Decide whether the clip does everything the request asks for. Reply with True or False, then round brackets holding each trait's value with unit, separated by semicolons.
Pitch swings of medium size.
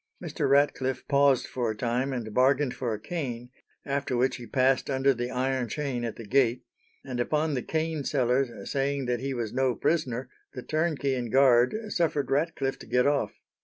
False (2.3 semitones)